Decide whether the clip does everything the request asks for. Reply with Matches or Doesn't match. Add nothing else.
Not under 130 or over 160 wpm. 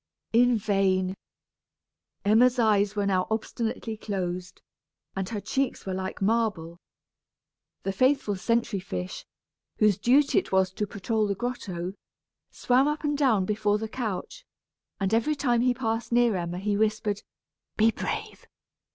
Matches